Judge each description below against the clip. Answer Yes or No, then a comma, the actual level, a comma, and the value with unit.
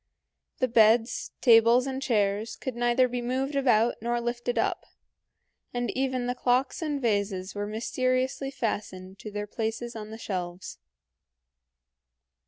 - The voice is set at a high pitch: Yes, high, 240 Hz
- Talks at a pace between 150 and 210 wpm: No, slow, 135 wpm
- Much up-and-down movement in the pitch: No, average, 3.1 semitones